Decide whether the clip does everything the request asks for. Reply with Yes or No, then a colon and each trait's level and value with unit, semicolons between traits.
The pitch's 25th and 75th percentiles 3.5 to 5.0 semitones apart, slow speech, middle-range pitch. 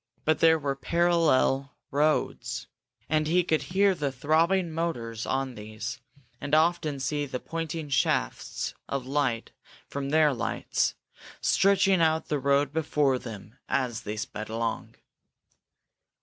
Yes: average, 3.8 semitones; slow, 130 wpm; medium, 145 Hz